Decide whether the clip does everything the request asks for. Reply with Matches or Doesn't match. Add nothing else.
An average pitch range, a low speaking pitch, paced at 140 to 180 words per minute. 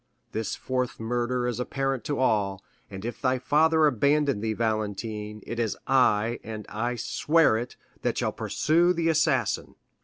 Matches